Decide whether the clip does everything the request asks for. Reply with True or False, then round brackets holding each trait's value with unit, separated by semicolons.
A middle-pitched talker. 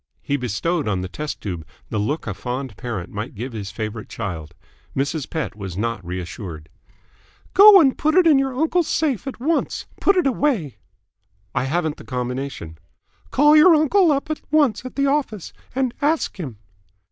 True (150 Hz)